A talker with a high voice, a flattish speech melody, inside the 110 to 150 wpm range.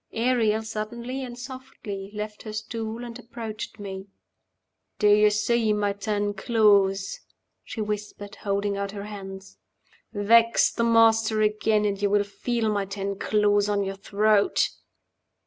Yes: high, 210 Hz; narrow, 1.9 semitones; average, 140 wpm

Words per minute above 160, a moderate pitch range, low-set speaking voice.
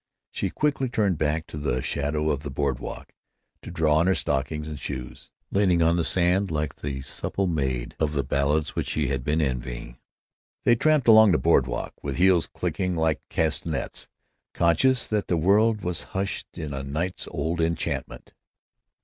Yes: average, 175 wpm; average, 4.5 semitones; very low, 80 Hz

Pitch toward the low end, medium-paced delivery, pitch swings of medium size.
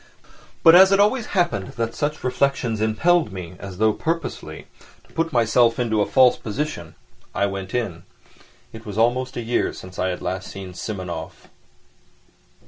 No: low, 115 Hz; average, 160 wpm; wide, 6.1 semitones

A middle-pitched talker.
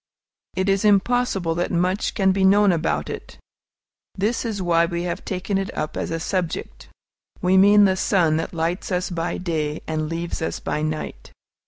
Yes: medium, 180 Hz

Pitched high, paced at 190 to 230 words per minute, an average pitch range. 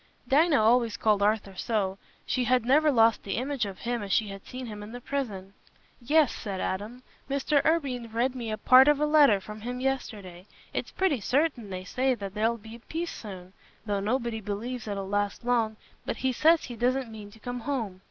Yes: high, 235 Hz; average, 200 wpm; average, 4.1 semitones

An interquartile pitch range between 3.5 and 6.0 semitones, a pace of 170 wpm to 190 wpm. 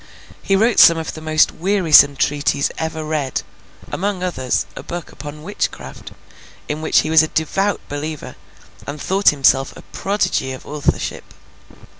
No: average, 4.0 semitones; average, 140 wpm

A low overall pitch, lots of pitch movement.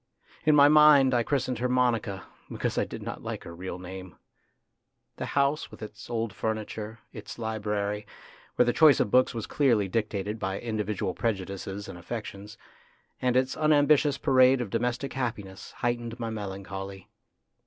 No: low, 115 Hz; average, 4.0 semitones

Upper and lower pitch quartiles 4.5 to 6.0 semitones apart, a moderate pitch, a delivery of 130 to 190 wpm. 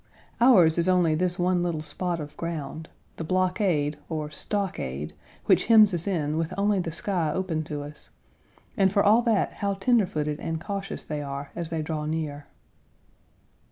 No: average, 4.0 semitones; medium, 170 Hz; average, 170 wpm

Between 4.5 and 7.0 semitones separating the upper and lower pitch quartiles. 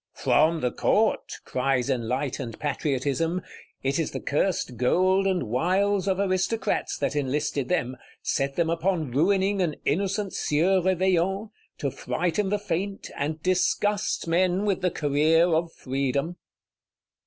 Yes: average, 5.2 semitones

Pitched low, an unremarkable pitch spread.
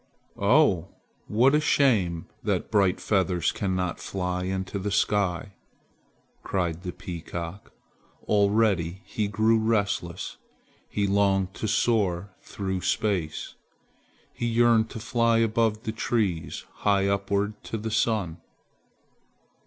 Yes: low, 100 Hz; average, 3.2 semitones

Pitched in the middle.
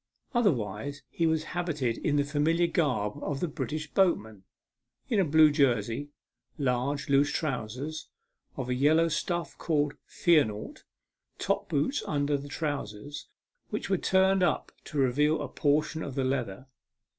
Yes: medium, 145 Hz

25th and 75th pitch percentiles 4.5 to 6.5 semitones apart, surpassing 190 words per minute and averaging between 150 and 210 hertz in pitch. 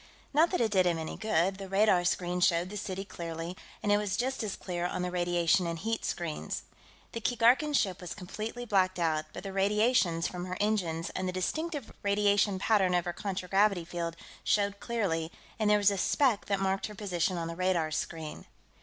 No: average, 3.1 semitones; average, 200 wpm; high, 190 Hz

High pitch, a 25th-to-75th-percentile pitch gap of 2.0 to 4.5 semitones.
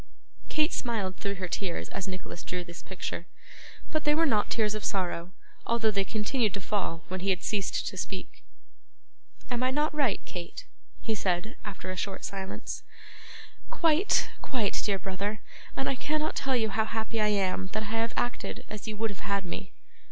Yes: high, 210 Hz; average, 3.9 semitones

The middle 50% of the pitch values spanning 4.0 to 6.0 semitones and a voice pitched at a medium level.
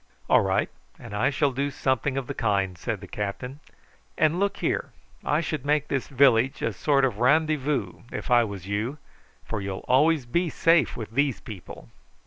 No: wide, 5.4 semitones; low, 130 Hz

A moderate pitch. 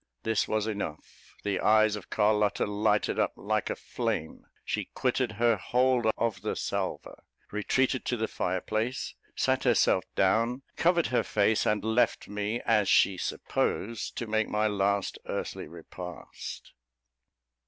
No: low, 110 Hz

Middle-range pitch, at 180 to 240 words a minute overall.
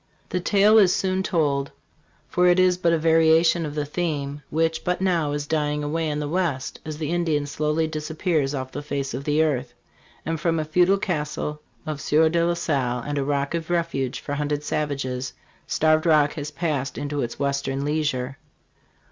Yes: medium, 150 Hz; average, 185 wpm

